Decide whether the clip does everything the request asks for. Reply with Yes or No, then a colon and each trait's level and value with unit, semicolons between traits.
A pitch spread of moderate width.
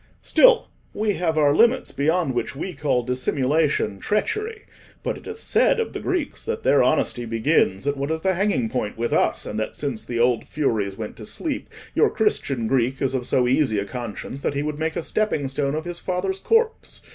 No: wide, 7.7 semitones